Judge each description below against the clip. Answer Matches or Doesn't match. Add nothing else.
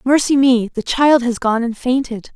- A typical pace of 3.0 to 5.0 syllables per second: Matches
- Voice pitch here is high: Matches